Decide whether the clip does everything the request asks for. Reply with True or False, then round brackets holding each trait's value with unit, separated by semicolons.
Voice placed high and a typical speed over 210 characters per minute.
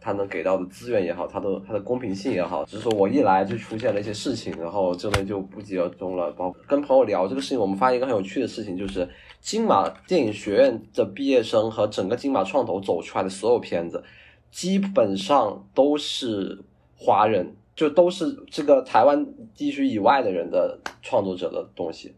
False (135 Hz; 320 characters per minute)